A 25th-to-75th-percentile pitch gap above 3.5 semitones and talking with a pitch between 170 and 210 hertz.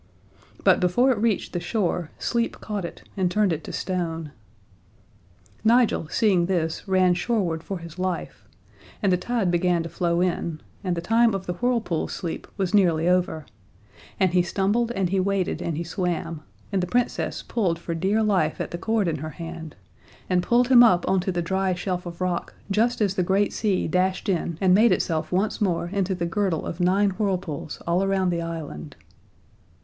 No: average, 2.9 semitones; medium, 185 Hz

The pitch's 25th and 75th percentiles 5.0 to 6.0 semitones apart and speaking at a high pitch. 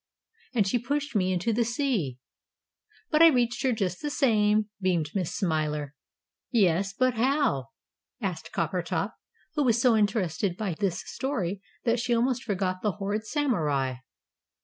Yes: average, 5.3 semitones; high, 210 Hz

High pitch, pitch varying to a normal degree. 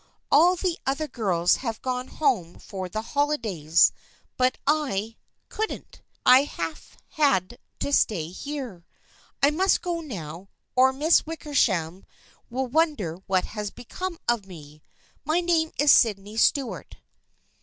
No: very high, 250 Hz; wide, 7.8 semitones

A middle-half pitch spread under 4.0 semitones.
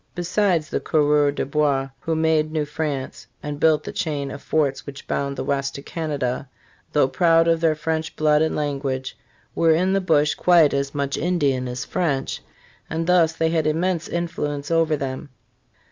Yes: narrow, 2.6 semitones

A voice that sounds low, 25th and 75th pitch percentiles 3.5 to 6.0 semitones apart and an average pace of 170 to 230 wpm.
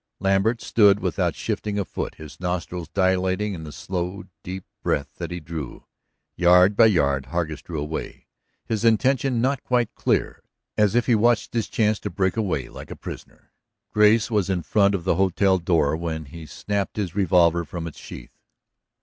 Yes: very low, 95 Hz; average, 3.9 semitones; average, 175 wpm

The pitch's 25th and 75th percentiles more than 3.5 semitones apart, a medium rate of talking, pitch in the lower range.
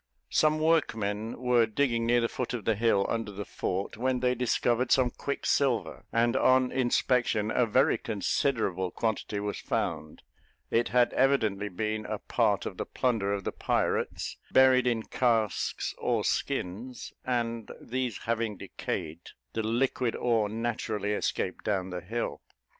No: average, 3.2 semitones; average, 145 wpm; low, 115 Hz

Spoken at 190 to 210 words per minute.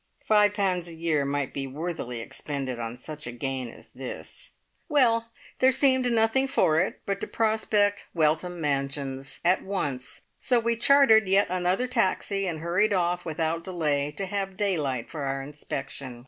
No: average, 160 wpm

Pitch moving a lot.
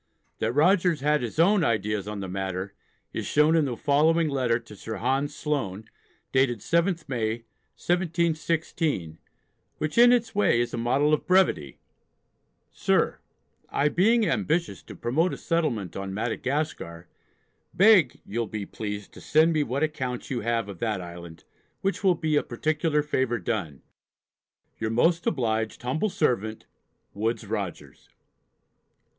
Yes: wide, 6.7 semitones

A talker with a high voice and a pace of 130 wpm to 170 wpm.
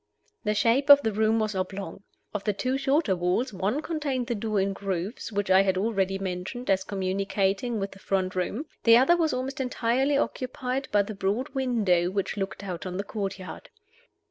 No: high, 205 Hz; average, 190 wpm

